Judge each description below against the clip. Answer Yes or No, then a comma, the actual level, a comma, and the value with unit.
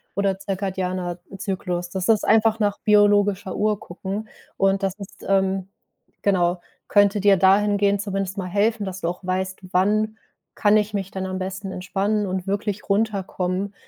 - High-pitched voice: Yes, high, 195 Hz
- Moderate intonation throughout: No, narrow, 1.6 semitones